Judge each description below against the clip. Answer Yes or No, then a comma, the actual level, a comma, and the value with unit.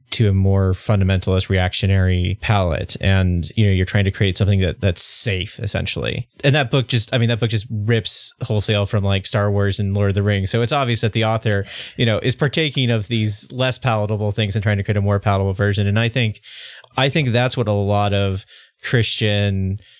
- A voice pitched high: No, low, 105 Hz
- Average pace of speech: No, fast, 215 wpm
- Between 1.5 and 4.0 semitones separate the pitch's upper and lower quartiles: Yes, average, 2.9 semitones